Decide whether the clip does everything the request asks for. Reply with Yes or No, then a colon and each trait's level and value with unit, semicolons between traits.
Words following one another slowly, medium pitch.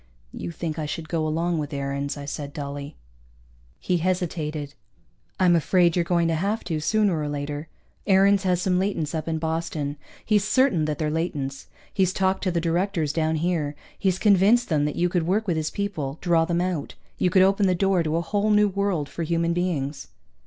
No: average, 200 wpm; medium, 170 Hz